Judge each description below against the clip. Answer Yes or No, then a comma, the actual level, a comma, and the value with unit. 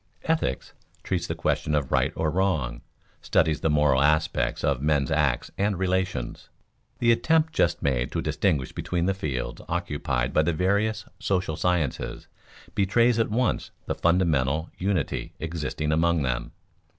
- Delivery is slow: No, average, 145 wpm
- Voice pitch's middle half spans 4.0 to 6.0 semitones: Yes, average, 5.1 semitones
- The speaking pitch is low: Yes, very low, 80 Hz